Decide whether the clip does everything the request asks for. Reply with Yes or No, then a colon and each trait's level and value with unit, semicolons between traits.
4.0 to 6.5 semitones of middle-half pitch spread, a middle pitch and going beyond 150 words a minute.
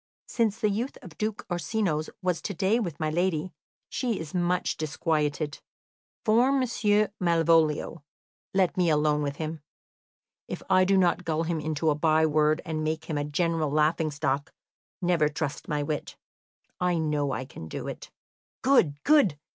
No: average, 3.6 semitones; medium, 160 Hz; average, 160 wpm